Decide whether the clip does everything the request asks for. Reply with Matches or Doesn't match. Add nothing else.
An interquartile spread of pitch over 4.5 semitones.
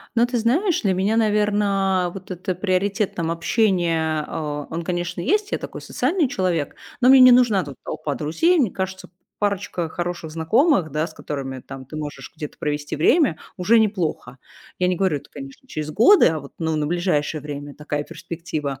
Matches